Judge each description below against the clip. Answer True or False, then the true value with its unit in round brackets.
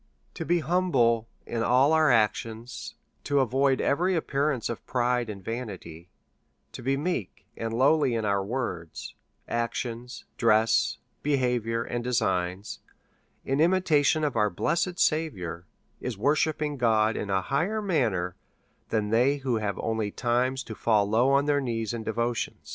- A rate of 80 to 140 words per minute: False (150 wpm)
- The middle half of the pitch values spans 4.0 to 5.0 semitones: True (4.3 semitones)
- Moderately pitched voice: False (120 Hz)